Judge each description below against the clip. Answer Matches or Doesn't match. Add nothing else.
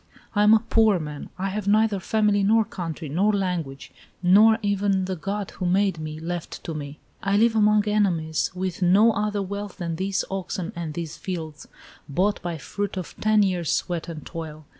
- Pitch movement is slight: Doesn't match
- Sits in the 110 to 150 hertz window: Doesn't match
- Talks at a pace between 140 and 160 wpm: Doesn't match